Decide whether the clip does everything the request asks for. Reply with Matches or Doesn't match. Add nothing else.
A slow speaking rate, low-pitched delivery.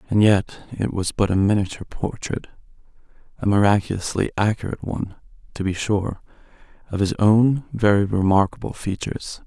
Matches